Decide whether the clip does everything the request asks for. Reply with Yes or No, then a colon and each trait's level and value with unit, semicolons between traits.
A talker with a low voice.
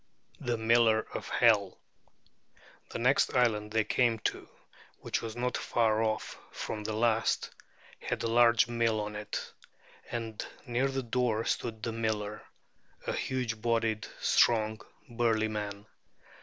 Yes: low, 115 Hz